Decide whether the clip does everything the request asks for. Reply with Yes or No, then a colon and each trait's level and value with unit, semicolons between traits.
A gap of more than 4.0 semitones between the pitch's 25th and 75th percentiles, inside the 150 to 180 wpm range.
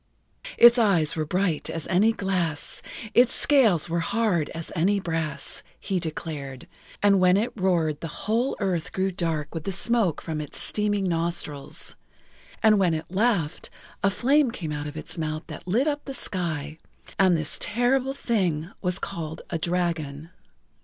Yes: average, 4.6 semitones; average, 160 wpm